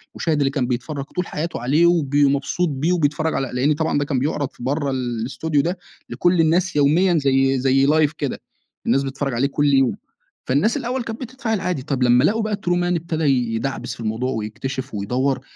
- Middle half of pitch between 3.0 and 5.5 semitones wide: Yes, average, 4.1 semitones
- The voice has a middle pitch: Yes, medium, 145 Hz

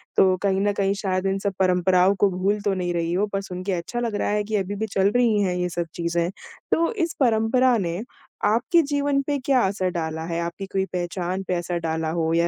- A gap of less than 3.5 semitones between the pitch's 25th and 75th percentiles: Yes, average, 3.1 semitones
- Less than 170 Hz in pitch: No, high, 195 Hz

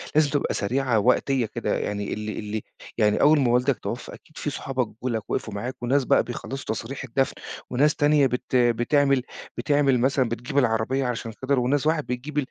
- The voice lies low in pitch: Yes, low, 130 Hz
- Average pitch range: Yes, average, 3.0 semitones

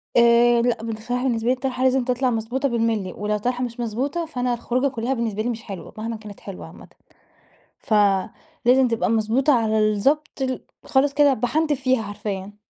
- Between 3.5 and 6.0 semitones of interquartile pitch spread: No, average, 3.0 semitones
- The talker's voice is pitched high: Yes, high, 240 Hz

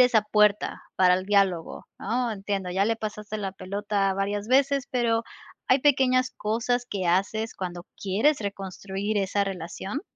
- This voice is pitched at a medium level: No, high, 205 Hz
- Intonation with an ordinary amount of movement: Yes, average, 3.1 semitones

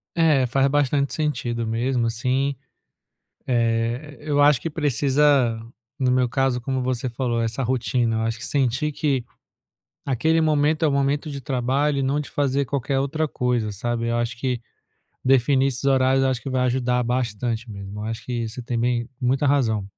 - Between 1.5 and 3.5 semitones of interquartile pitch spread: Yes, average, 2.9 semitones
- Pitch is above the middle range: No, low, 130 Hz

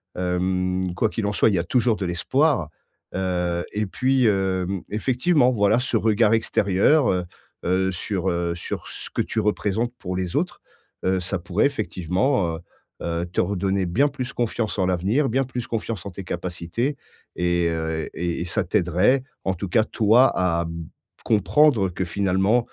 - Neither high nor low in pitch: No, very low, 95 Hz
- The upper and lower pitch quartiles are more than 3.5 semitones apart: Yes, average, 4.3 semitones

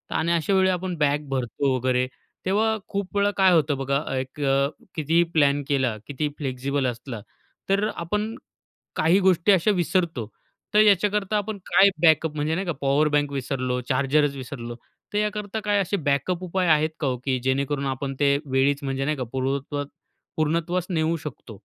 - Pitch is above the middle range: No, medium, 150 Hz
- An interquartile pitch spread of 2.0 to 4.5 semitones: No, average, 5.1 semitones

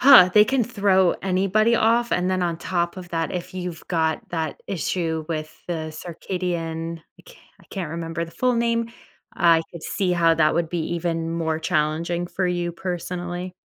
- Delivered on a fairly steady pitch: Yes, narrow, 2.2 semitones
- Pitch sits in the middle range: Yes, medium, 175 Hz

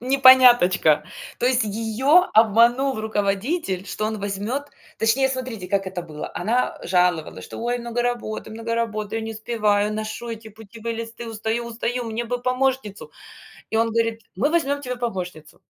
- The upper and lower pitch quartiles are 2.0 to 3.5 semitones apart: Yes, average, 2.7 semitones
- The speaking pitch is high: Yes, high, 225 Hz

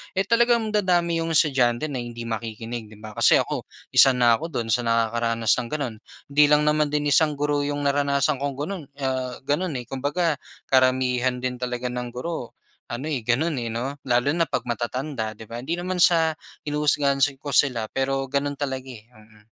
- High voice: No, low, 135 Hz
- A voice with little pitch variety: No, average, 3.7 semitones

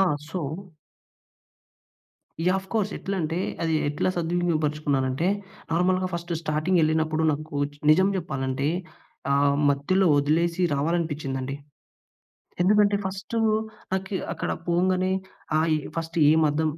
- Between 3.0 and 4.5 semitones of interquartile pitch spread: Yes, average, 3.7 semitones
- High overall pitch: No, medium, 165 Hz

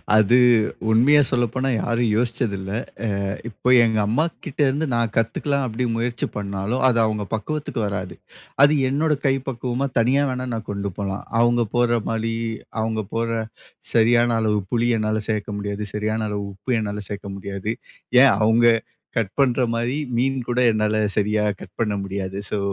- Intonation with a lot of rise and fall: No, average, 2.8 semitones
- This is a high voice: No, low, 115 Hz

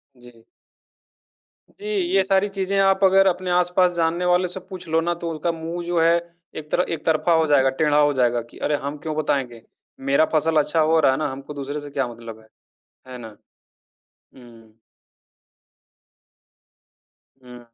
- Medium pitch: Yes, medium, 155 Hz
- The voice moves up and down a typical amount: Yes, average, 5.0 semitones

